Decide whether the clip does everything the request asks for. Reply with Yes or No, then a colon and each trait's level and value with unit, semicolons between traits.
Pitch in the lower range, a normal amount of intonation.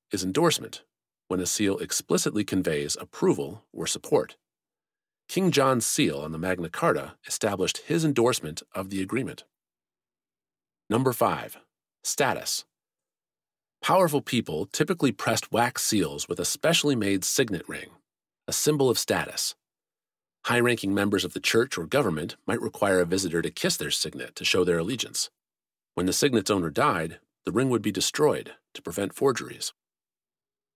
No: very low, 95 Hz; wide, 7.8 semitones